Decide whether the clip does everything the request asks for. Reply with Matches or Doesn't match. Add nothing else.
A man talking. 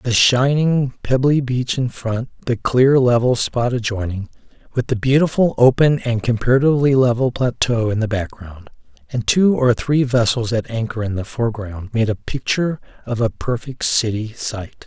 Matches